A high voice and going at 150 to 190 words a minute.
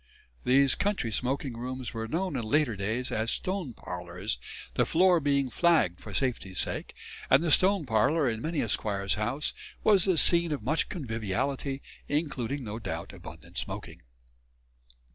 No: low, 130 Hz; average, 155 wpm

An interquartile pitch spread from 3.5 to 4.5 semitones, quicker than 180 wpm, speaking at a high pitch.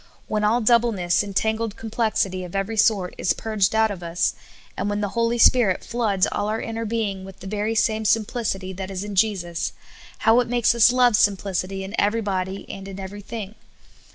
No: average, 2.8 semitones; average, 190 wpm; high, 205 Hz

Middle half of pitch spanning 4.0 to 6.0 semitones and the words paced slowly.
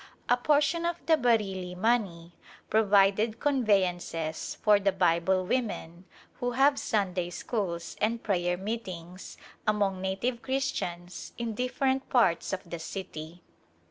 Yes: average, 5.3 semitones; slow, 120 wpm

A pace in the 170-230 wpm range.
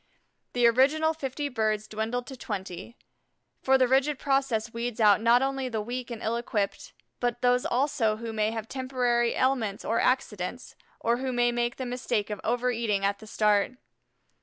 Yes: average, 175 wpm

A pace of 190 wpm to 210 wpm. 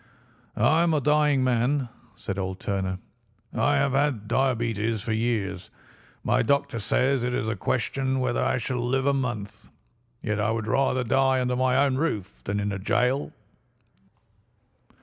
No: average, 160 wpm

